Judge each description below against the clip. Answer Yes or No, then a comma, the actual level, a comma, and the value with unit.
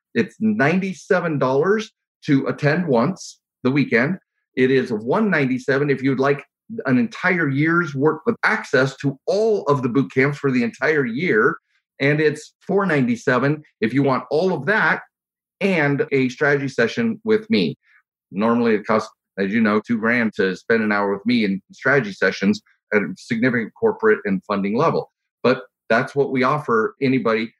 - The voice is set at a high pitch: No, medium, 140 Hz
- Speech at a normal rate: Yes, average, 160 wpm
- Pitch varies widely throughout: Yes, wide, 7.6 semitones